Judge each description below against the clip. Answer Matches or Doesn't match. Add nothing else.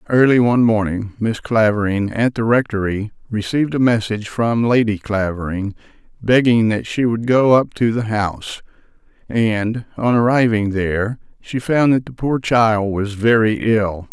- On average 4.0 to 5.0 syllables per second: Matches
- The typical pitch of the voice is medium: Doesn't match